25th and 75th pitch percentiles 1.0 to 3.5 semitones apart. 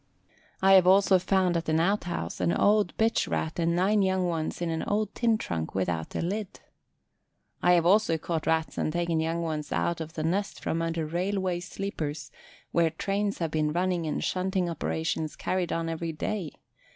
Yes: average, 2.9 semitones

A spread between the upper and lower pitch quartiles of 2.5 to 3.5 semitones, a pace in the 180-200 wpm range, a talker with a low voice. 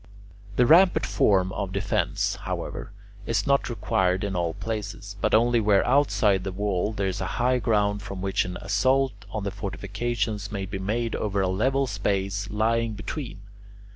No: average, 3.0 semitones; average, 165 wpm; low, 105 Hz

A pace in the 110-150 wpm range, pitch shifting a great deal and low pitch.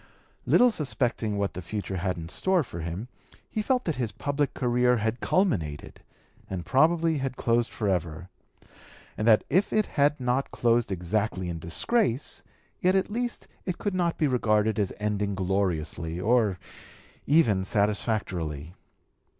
Yes: average, 145 wpm; wide, 7.5 semitones; low, 110 Hz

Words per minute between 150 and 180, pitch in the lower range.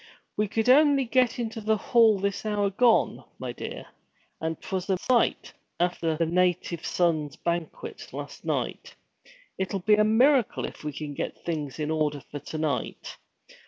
No: average, 160 wpm; high, 190 Hz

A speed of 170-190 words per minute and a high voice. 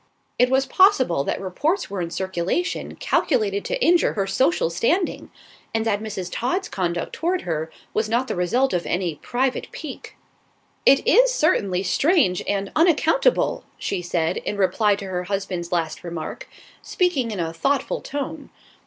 No: average, 155 wpm; high, 210 Hz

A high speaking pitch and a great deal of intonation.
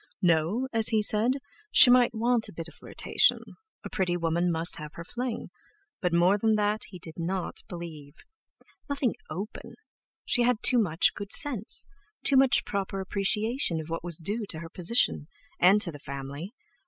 Yes: high, 195 Hz; wide, 5.8 semitones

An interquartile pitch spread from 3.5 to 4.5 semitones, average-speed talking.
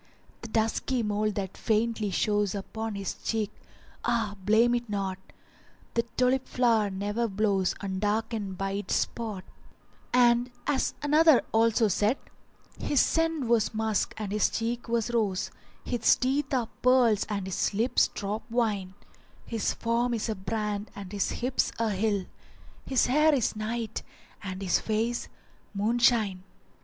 No: average, 2.8 semitones; average, 150 wpm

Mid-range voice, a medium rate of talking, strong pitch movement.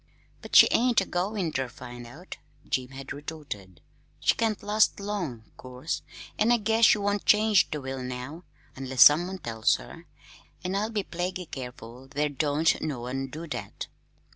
Yes: medium, 155 Hz; average, 170 wpm; wide, 7.4 semitones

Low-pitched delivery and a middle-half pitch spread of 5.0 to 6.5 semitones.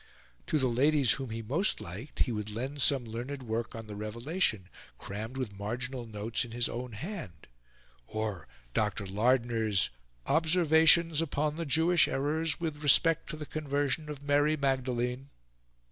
Yes: low, 130 Hz; average, 5.3 semitones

